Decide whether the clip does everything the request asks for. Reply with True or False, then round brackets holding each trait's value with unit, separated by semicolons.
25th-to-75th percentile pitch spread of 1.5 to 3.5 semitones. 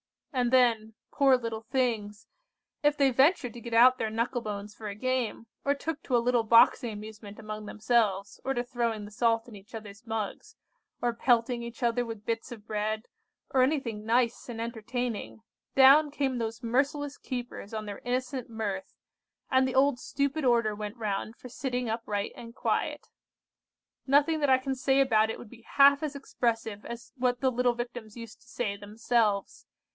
True (2.9 semitones)